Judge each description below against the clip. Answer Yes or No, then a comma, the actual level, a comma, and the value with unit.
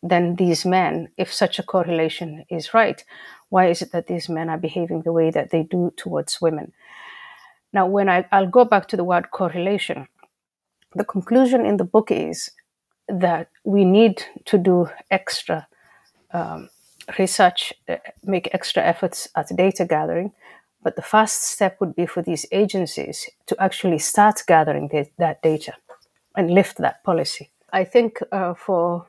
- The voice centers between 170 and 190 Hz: Yes, medium, 185 Hz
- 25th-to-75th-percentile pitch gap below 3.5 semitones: Yes, average, 2.8 semitones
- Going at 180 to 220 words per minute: No, average, 165 wpm